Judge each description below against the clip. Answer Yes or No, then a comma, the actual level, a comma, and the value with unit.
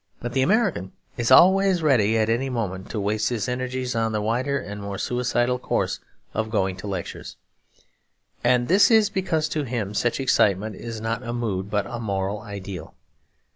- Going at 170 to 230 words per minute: Yes, average, 175 wpm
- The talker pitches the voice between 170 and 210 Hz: No, low, 115 Hz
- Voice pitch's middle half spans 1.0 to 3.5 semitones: No, average, 4.0 semitones